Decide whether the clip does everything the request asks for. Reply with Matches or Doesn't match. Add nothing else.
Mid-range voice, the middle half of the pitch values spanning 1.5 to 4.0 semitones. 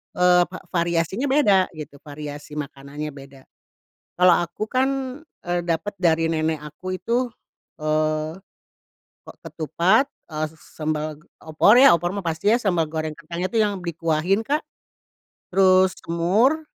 Matches